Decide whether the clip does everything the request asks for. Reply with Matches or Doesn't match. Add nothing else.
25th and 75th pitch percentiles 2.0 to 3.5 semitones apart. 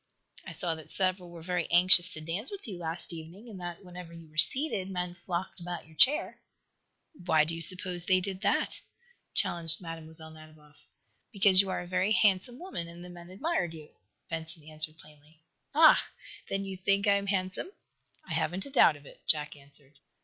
Matches